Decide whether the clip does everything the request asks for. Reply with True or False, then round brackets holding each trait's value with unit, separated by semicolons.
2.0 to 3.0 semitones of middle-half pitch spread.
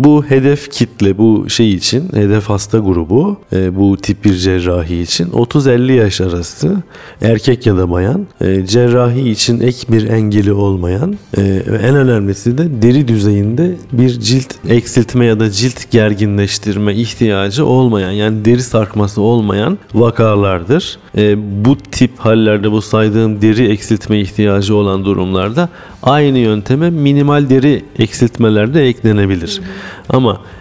False (3.8 semitones)